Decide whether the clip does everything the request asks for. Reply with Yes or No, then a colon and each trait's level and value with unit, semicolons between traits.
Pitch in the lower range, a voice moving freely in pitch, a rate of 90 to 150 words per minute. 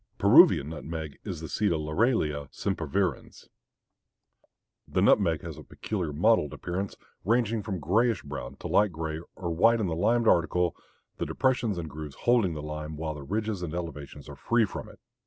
No: very low, 85 Hz; wide, 5.9 semitones; average, 175 wpm